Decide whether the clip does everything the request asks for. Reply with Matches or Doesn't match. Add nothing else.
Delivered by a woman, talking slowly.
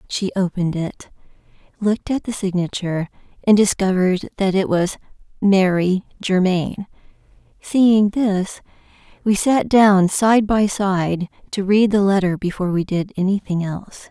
Matches